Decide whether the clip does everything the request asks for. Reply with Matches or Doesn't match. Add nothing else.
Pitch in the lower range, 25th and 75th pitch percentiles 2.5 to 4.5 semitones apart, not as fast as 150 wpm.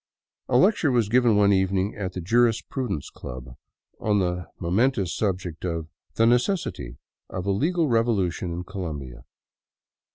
Doesn't match